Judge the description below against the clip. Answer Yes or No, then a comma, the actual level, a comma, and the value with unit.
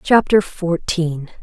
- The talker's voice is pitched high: No, medium, 175 Hz